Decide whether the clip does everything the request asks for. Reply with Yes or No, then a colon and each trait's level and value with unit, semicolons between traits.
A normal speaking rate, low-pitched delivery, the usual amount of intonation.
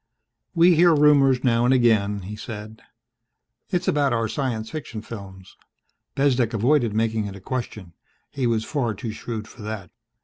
Yes: average, 160 wpm; low, 115 Hz; average, 3.8 semitones